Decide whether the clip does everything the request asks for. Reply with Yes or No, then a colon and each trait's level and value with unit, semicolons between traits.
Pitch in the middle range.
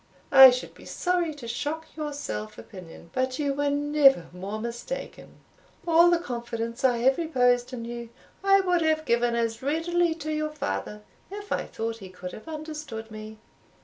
No: very high, 265 Hz